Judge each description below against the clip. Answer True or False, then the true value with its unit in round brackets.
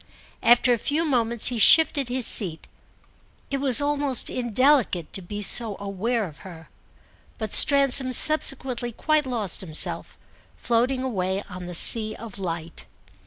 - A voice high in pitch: True (235 Hz)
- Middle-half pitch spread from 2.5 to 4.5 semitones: False (5.3 semitones)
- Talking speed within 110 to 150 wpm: True (140 wpm)